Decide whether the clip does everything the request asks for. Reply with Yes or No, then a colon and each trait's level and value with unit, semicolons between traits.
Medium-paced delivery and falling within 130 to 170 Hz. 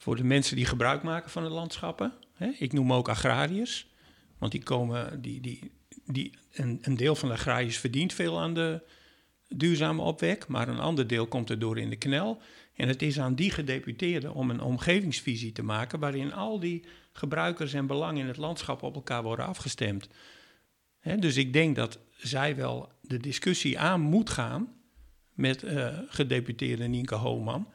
Yes: average, 170 wpm; medium, 140 Hz